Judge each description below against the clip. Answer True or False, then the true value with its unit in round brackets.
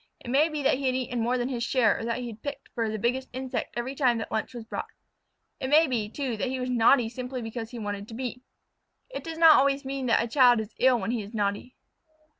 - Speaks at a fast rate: True (260 wpm)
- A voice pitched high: True (245 Hz)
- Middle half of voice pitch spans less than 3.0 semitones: True (2.6 semitones)